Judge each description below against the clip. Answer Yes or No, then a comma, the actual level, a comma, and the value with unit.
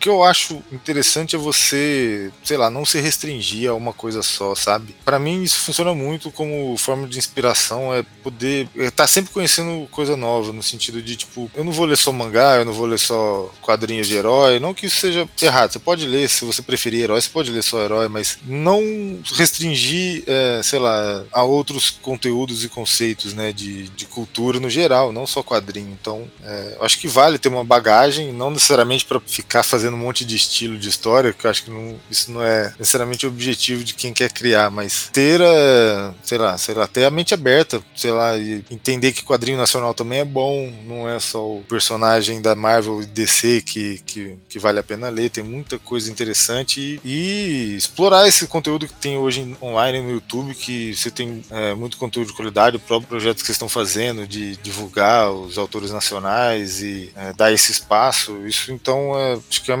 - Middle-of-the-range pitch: No, low, 120 Hz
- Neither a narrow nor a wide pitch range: Yes, average, 3.9 semitones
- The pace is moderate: No, fast, 205 wpm